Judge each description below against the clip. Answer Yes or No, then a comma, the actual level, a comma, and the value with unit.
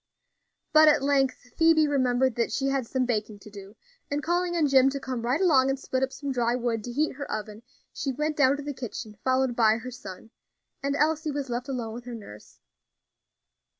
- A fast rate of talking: Yes, fast, 210 wpm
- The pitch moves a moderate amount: Yes, average, 3.3 semitones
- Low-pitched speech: No, very high, 260 Hz